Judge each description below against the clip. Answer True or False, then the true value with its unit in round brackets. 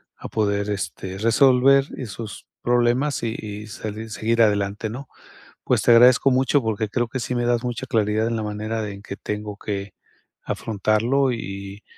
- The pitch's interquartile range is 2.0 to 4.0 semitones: True (2.7 semitones)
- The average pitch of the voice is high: False (110 Hz)